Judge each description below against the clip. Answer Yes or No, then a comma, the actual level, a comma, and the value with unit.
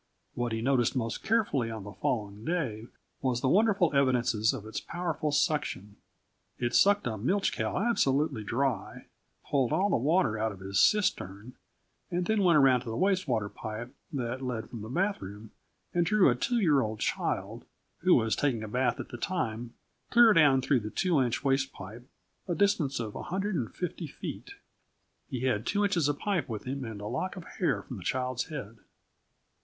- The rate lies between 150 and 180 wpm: No, average, 190 wpm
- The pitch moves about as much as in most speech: No, wide, 7.3 semitones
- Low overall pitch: Yes, low, 130 Hz